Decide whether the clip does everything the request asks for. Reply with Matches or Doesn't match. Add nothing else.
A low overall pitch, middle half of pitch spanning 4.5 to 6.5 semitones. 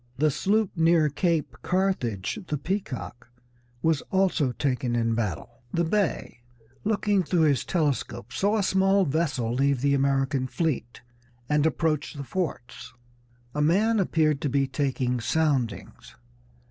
Doesn't match